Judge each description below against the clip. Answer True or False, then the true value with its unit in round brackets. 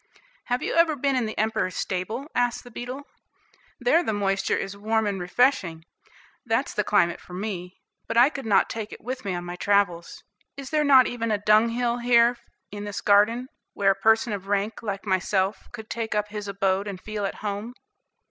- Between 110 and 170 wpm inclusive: False (195 wpm)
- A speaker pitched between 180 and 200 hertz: False (215 Hz)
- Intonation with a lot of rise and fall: False (3.5 semitones)